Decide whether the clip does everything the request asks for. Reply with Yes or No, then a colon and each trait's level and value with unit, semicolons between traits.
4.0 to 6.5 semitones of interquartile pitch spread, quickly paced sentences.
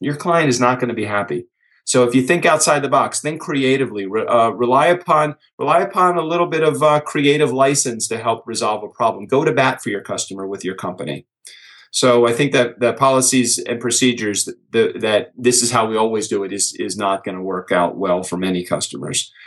Yes: average, 5.1 semitones; fast, 220 wpm